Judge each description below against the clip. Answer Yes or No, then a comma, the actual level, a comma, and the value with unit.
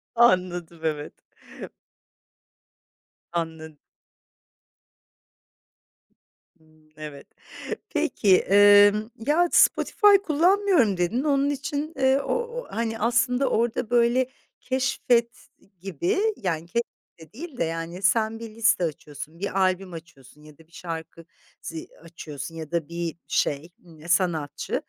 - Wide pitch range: Yes, wide, 7.1 semitones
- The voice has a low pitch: No, medium, 185 Hz